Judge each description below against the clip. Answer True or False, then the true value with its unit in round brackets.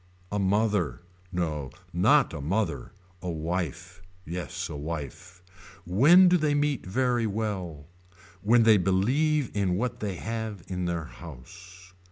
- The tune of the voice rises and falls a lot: False (4.5 semitones)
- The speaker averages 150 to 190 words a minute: False (135 wpm)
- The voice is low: True (95 Hz)